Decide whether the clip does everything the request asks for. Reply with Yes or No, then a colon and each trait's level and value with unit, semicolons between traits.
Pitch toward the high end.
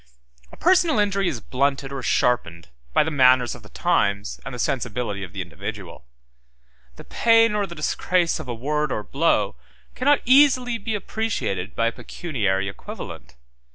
No: medium, 140 Hz